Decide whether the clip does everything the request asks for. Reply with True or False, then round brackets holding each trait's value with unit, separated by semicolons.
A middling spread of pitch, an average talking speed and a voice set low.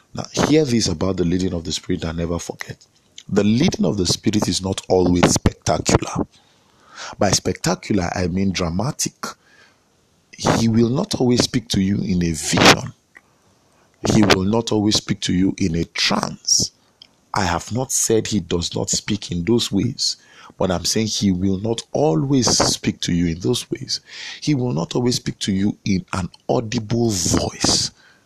True (4.3 semitones; 170 wpm; 100 Hz)